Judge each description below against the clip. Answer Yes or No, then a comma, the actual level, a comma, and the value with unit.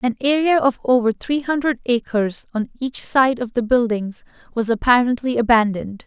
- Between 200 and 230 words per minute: No, average, 160 wpm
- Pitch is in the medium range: No, high, 245 Hz